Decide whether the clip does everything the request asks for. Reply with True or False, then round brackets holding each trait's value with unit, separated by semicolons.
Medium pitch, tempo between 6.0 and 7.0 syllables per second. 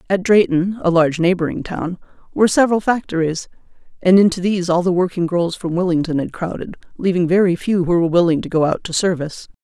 True (180 Hz; 6.3 syllables/s)